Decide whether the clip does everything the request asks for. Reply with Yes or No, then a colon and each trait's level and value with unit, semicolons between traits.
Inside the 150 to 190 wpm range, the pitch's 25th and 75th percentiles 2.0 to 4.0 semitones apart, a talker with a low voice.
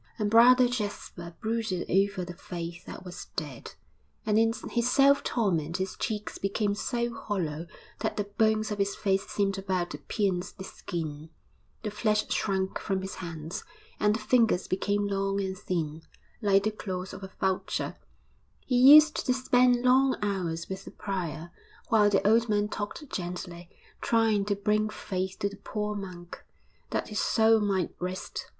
No: average, 165 wpm; average, 3.0 semitones; high, 200 Hz